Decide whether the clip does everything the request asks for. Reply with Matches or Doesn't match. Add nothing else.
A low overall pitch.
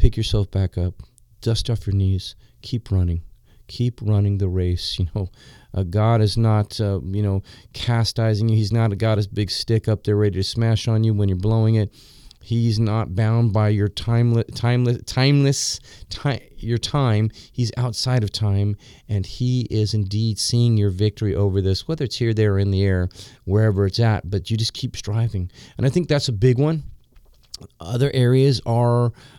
Matches